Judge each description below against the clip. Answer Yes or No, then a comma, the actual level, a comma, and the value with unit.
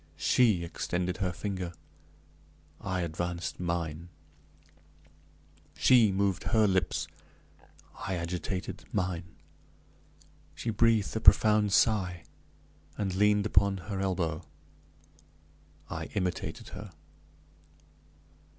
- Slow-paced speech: Yes, slow, 85 wpm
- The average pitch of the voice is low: Yes, very low, 95 Hz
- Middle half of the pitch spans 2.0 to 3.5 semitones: Yes, average, 2.9 semitones